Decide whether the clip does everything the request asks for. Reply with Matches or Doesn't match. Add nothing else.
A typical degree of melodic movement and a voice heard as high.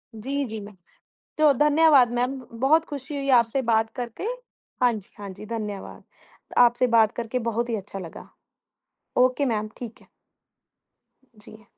Matches